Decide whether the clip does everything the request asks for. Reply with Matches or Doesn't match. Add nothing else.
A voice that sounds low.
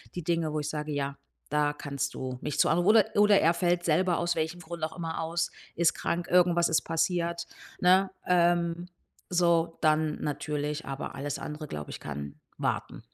Doesn't match